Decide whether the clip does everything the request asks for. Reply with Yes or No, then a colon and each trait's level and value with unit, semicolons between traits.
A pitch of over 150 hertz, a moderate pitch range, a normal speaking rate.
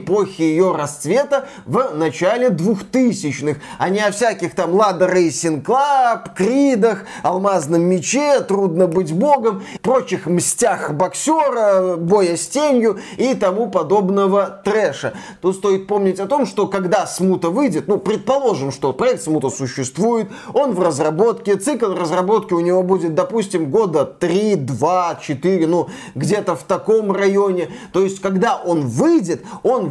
Yes: high, 190 Hz; average, 4.0 semitones; average, 140 wpm